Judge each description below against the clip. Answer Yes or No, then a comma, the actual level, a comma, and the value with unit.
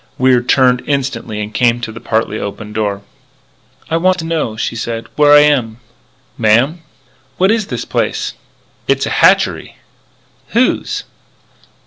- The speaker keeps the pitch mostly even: No, average, 5.0 semitones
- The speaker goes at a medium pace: Yes, average, 145 wpm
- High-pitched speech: No, low, 125 Hz